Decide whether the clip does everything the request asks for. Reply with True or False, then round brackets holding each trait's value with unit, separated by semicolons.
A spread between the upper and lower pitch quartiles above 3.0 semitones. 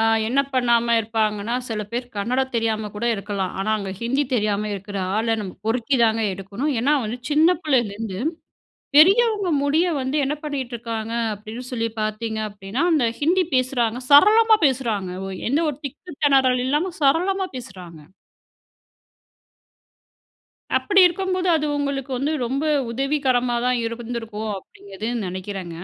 True (5.0 semitones)